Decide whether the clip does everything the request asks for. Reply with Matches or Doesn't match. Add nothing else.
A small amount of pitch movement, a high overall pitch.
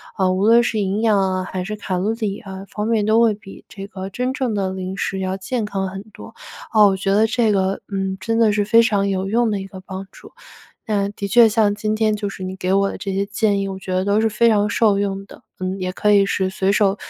Matches